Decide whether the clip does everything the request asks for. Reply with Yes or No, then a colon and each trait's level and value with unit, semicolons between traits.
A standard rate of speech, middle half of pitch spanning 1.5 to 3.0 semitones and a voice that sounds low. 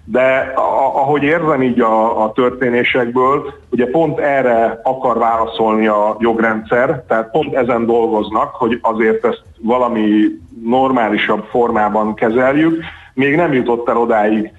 Yes: average, 125 wpm; average, 2.7 semitones; low, 115 Hz